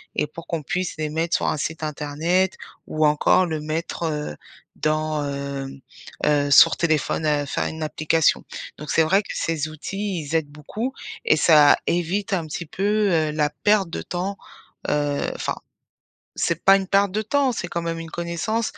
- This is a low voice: No, medium, 160 Hz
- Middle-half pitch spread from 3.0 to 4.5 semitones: Yes, average, 3.7 semitones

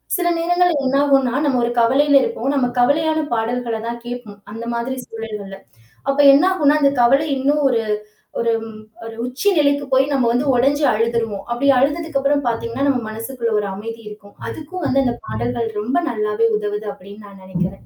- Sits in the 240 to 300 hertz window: Yes, high, 245 Hz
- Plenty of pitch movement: No, average, 4.0 semitones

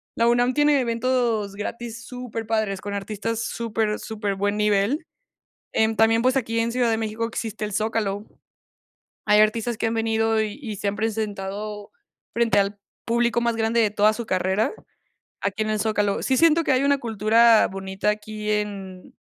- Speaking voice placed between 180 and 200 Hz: No, high, 220 Hz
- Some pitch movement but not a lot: No, narrow, 1.9 semitones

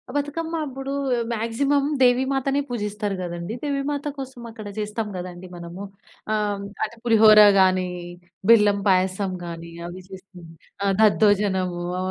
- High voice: Yes, high, 210 Hz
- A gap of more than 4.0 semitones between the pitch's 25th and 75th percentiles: Yes, wide, 5.6 semitones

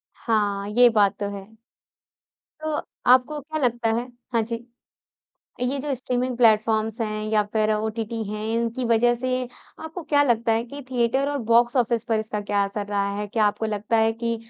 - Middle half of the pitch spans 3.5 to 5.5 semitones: No, narrow, 2.5 semitones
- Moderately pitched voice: No, high, 230 Hz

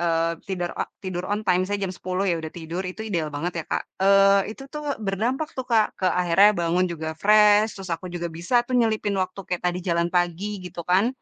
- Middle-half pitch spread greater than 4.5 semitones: No, average, 3.0 semitones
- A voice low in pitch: No, medium, 185 Hz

